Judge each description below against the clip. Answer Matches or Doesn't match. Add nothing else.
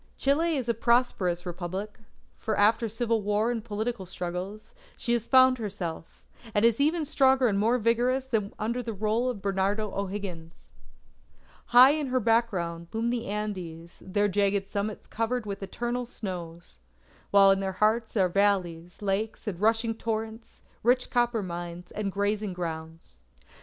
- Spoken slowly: Doesn't match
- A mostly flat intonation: Doesn't match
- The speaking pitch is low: Doesn't match